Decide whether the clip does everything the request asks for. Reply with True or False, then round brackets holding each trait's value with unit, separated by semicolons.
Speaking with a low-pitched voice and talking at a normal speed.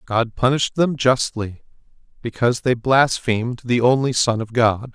True (120 Hz; 145 wpm)